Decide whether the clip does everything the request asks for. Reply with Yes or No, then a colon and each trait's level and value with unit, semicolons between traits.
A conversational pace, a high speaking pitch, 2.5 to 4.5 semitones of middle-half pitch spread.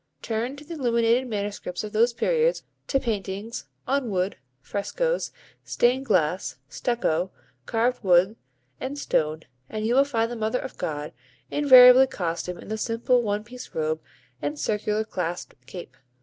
No: average, 150 wpm; high, 220 Hz; wide, 5.4 semitones